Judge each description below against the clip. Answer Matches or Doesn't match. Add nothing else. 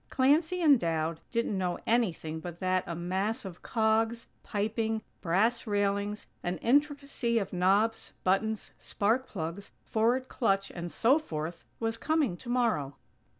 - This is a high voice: Matches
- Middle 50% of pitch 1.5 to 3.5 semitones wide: Doesn't match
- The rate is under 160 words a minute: Matches